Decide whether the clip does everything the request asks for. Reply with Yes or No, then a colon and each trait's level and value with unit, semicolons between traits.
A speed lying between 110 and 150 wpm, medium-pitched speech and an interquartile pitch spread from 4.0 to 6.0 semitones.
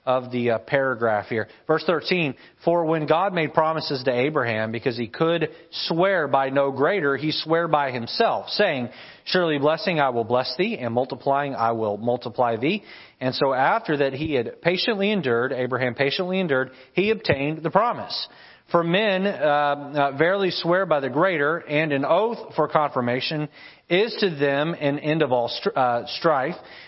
No: average, 170 wpm; medium, 150 Hz; average, 4.8 semitones